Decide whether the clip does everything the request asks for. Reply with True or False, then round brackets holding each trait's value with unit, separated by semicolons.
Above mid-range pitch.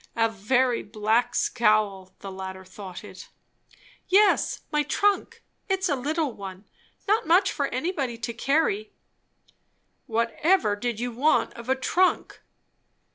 True (240 Hz)